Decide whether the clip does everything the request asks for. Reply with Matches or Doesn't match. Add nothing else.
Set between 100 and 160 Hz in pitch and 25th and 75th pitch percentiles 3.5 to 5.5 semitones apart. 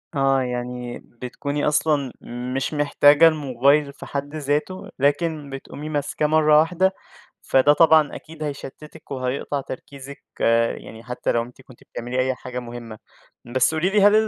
Doesn't match